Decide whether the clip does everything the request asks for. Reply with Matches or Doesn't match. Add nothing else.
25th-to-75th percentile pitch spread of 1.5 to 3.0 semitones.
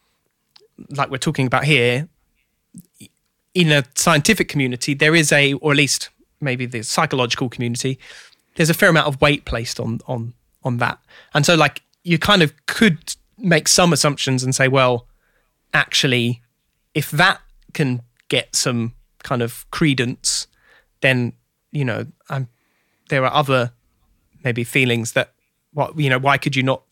Doesn't match